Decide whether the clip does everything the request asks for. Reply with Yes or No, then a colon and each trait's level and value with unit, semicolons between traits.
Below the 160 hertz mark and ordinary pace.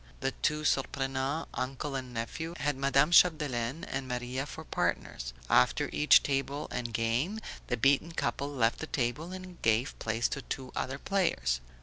Yes: low, 135 Hz; average, 145 wpm